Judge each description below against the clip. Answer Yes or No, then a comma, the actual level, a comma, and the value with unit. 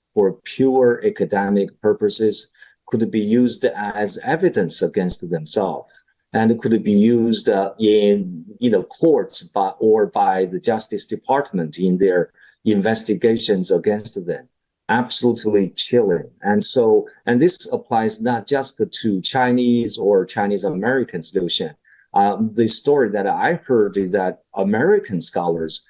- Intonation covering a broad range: No, average, 2.8 semitones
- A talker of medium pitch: No, low, 110 Hz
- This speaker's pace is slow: Yes, slow, 130 wpm